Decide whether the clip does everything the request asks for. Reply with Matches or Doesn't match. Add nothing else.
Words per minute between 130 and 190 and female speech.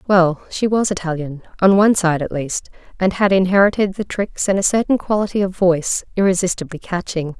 Matches